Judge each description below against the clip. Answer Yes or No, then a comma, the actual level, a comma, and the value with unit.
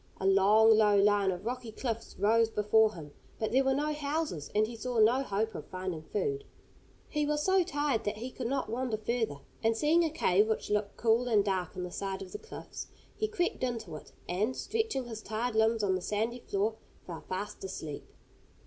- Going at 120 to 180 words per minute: No, fast, 205 wpm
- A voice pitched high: Yes, high, 220 Hz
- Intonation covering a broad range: No, average, 4.3 semitones